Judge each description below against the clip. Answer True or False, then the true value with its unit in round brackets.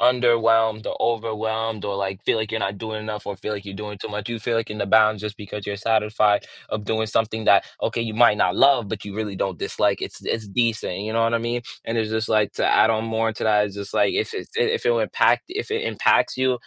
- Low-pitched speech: True (110 Hz)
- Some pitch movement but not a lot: False (1.8 semitones)